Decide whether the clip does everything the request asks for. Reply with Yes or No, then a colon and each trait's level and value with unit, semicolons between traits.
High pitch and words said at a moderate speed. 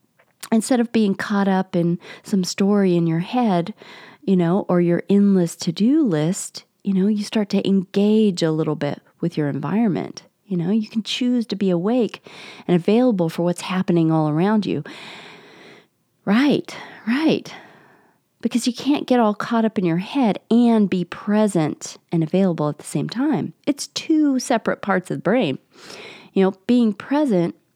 Yes: high, 200 Hz; average, 170 wpm